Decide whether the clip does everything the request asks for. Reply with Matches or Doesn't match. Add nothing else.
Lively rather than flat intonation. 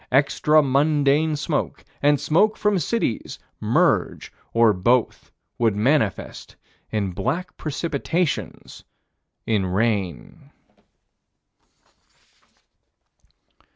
Matches